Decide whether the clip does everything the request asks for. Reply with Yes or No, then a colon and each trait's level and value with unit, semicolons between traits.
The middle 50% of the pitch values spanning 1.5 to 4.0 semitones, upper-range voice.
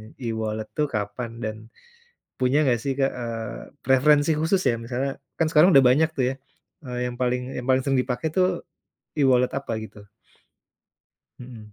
No: average, 3.4 semitones; low, 130 Hz